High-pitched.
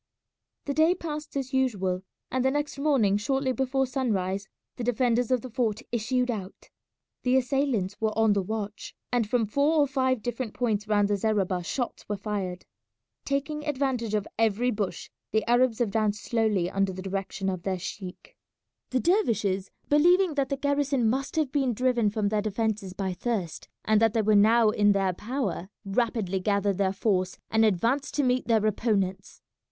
Yes: high, 225 Hz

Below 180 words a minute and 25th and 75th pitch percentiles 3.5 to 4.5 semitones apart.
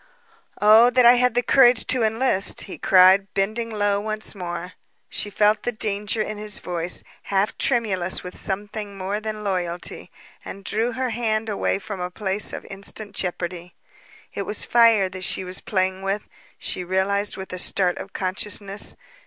No: average, 170 wpm; narrow, 2.5 semitones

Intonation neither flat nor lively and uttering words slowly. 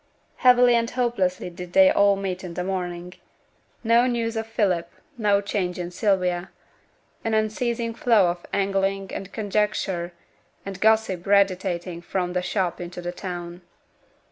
No: average, 3.6 semitones; average, 145 wpm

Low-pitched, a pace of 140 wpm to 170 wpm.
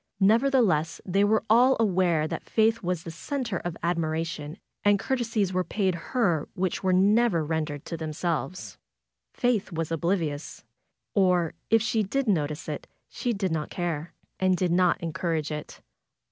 No: medium, 180 Hz; average, 150 wpm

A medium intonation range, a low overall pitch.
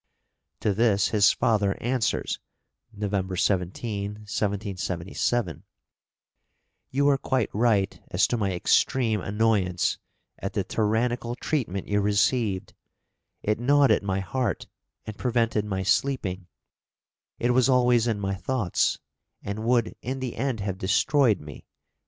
Yes: average, 3.7 semitones; low, 105 Hz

